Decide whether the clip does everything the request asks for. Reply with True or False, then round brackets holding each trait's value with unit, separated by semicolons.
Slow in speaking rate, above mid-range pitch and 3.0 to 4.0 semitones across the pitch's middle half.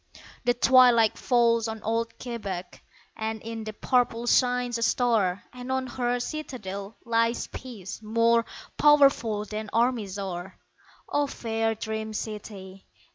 False (130 wpm; 230 Hz; 2.4 semitones)